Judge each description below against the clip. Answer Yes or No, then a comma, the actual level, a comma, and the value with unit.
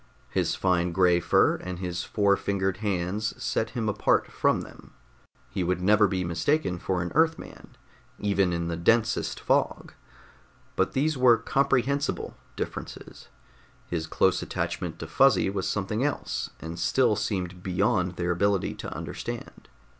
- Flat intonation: No, average, 3.8 semitones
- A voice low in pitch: Yes, very low, 95 Hz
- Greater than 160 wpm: No, average, 145 wpm